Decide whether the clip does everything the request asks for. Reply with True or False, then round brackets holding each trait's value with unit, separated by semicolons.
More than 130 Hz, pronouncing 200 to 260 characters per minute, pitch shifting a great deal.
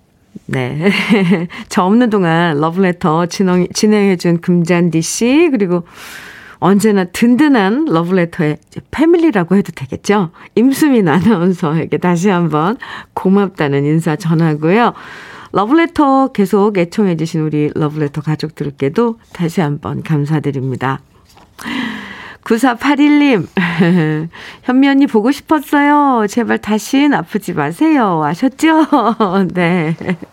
True (190 Hz; 240 characters per minute; 6.4 semitones)